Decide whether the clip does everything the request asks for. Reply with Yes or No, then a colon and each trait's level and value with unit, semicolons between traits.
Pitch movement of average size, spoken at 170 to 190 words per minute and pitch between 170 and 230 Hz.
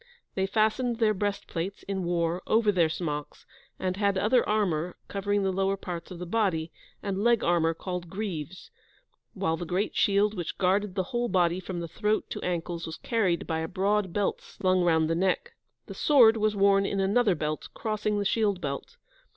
Yes: average, 3.3 semitones; average, 185 wpm; high, 190 Hz